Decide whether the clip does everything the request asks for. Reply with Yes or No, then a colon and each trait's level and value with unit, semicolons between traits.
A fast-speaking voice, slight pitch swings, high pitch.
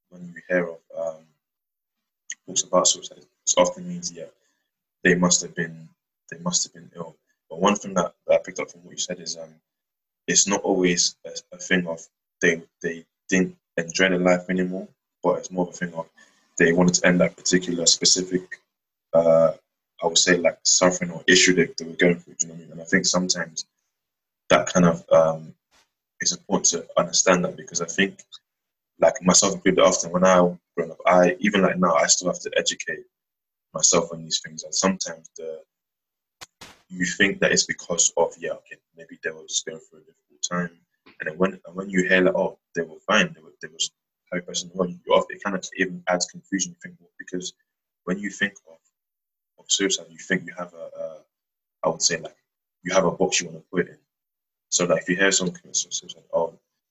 No: fast, 215 wpm; narrow, 2.1 semitones; very low, 90 Hz